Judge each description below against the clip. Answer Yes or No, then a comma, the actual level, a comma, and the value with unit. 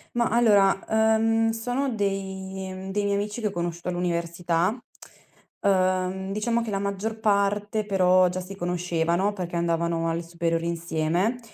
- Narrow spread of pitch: No, average, 3.3 semitones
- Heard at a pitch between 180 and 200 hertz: Yes, high, 190 Hz